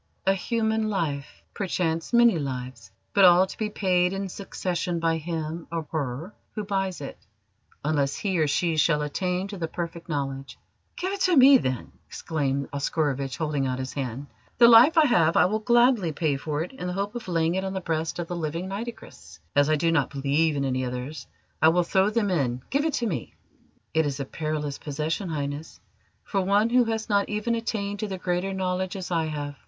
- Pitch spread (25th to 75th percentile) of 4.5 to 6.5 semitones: Yes, average, 5.3 semitones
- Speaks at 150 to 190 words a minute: No, fast, 205 wpm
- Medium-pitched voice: Yes, medium, 170 Hz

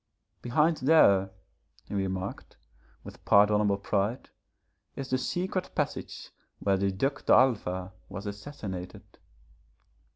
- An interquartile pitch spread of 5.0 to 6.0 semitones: Yes, wide, 5.5 semitones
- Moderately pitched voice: No, low, 105 Hz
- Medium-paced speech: No, slow, 100 wpm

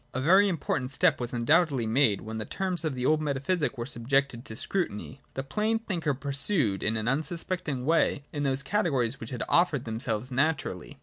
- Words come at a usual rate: Yes, average, 185 wpm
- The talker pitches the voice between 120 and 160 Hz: Yes, medium, 140 Hz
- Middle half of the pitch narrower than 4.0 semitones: No, average, 5.2 semitones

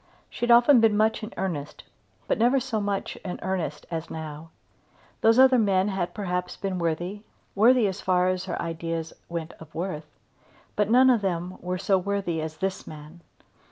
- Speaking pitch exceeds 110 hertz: Yes, high, 190 Hz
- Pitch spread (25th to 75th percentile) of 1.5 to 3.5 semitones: No, average, 4.2 semitones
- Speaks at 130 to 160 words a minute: No, average, 175 wpm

